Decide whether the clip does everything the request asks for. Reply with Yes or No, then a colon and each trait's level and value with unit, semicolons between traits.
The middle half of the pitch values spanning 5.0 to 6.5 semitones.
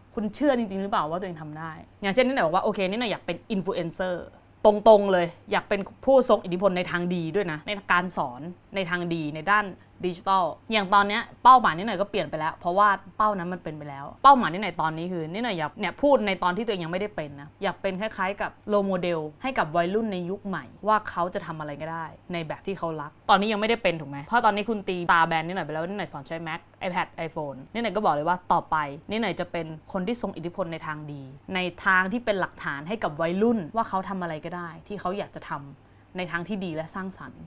No: average, 4.1 semitones